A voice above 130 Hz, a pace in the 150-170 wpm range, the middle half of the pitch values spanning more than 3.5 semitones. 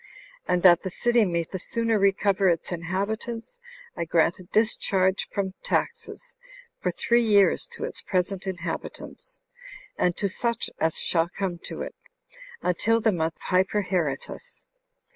No: high, 190 Hz; average, 140 wpm; average, 4.0 semitones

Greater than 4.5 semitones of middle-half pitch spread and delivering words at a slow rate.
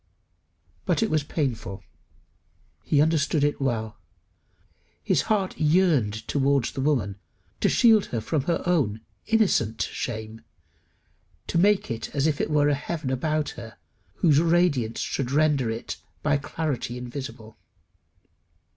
Yes: average, 5.3 semitones; slow, 125 wpm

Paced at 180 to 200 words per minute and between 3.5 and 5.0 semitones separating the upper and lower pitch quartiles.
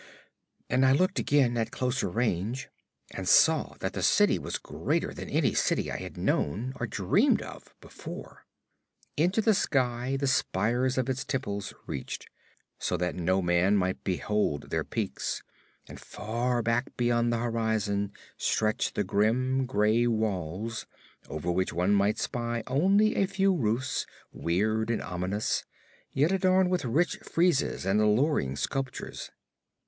No: average, 145 wpm; average, 4.6 semitones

